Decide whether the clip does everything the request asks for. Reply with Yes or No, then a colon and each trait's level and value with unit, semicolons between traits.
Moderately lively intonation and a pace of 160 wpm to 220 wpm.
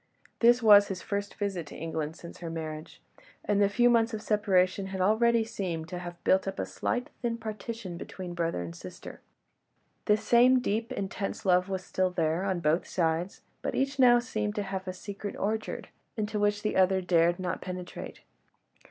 Yes: average, 3.4 semitones; average, 185 wpm